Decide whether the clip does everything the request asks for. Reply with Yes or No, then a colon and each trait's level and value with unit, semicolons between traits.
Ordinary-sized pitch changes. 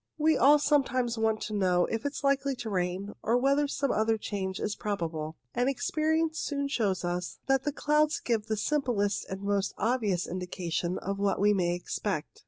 No: wide, 6.5 semitones